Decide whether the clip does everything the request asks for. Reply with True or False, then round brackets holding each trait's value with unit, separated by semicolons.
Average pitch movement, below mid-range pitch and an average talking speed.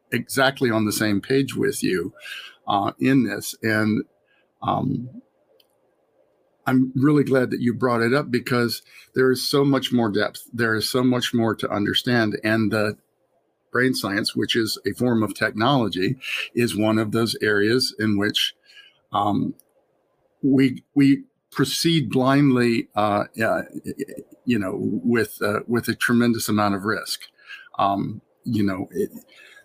True (3.4 semitones; 120 Hz; 145 wpm)